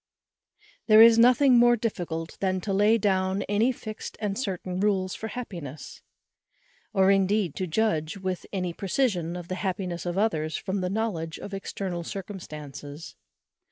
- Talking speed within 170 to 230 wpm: No, average, 155 wpm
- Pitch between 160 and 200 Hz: Yes, high, 190 Hz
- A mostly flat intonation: No, average, 3.5 semitones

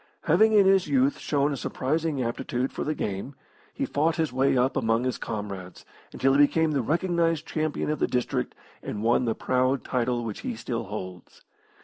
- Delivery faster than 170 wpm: Yes, average, 190 wpm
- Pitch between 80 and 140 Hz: Yes, low, 135 Hz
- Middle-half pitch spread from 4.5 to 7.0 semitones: Yes, average, 4.9 semitones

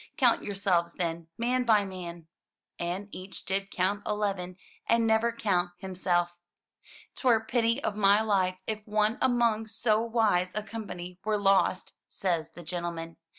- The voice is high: Yes, high, 200 Hz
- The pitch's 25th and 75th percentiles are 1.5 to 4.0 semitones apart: Yes, average, 3.6 semitones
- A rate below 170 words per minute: Yes, average, 155 wpm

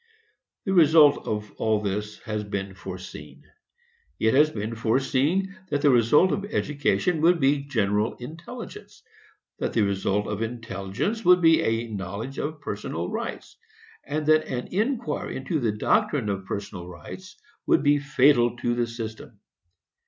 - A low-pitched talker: Yes, low, 120 Hz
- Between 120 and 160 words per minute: Yes, average, 145 wpm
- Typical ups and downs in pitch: No, wide, 6.7 semitones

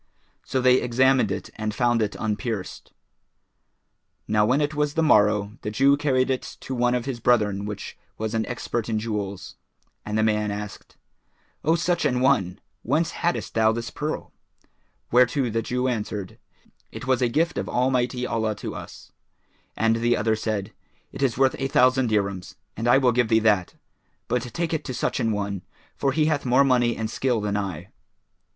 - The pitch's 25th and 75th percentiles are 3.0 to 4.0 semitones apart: Yes, average, 3.6 semitones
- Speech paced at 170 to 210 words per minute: Yes, average, 185 wpm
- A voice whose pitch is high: No, low, 120 Hz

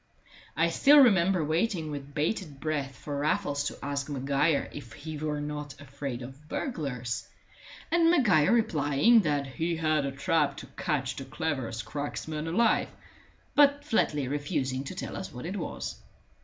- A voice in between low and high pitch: Yes, medium, 150 Hz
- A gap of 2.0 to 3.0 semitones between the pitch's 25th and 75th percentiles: No, average, 3.5 semitones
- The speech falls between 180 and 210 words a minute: No, average, 155 wpm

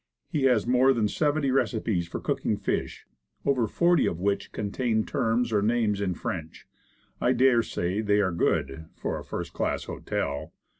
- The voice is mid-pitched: No, low, 110 Hz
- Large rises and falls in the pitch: No, average, 4.3 semitones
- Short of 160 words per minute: No, average, 165 wpm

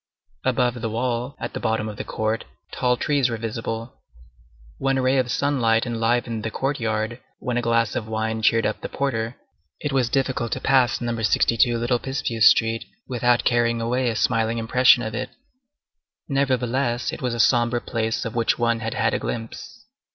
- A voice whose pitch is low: Yes, low, 120 Hz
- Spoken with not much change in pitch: Yes, narrow, 1.9 semitones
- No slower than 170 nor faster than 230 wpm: Yes, average, 180 wpm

